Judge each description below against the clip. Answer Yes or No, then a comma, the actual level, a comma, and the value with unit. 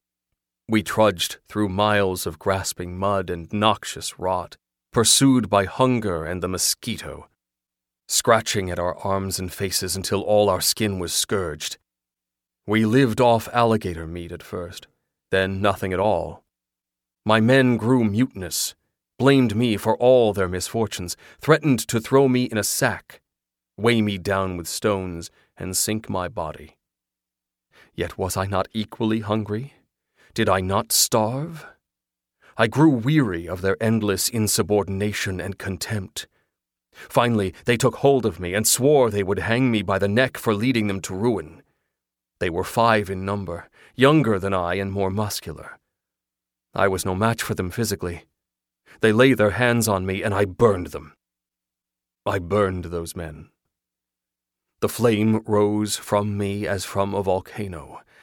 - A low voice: Yes, low, 100 Hz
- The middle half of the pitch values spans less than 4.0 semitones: No, average, 4.3 semitones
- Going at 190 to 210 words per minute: No, average, 150 wpm